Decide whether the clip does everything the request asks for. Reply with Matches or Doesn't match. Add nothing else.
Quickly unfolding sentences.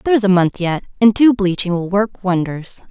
Matches